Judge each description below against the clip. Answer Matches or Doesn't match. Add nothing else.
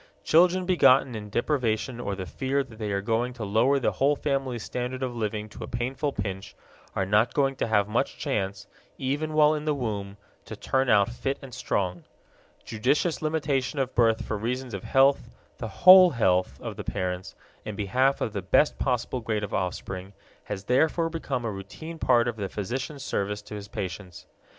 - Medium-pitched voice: Doesn't match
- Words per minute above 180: Matches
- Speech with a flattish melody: Doesn't match